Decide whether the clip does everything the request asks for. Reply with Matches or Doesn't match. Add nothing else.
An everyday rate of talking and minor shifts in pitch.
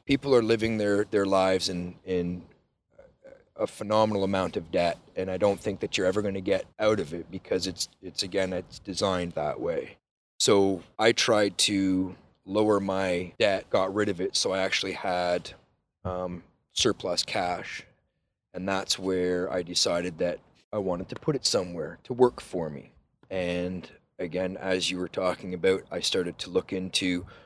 Matches